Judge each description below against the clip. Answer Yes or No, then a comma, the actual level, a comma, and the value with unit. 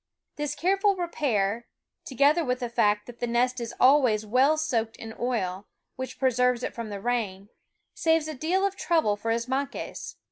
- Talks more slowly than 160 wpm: No, average, 175 wpm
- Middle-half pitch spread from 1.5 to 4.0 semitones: No, average, 4.8 semitones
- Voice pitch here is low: No, very high, 250 Hz